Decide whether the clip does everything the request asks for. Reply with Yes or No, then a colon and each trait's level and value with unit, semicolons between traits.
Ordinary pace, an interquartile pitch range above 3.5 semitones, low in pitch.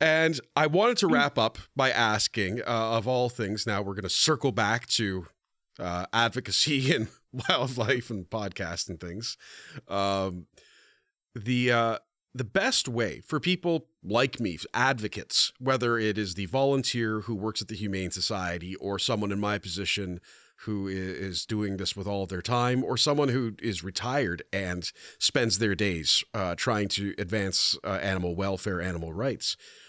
Yes: average, 165 wpm; average, 4.1 semitones; low, 105 Hz